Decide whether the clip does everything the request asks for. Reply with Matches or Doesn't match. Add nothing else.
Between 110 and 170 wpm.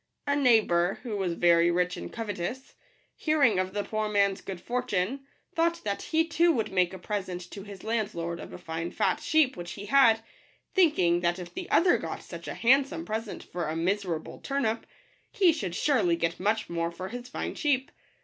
Doesn't match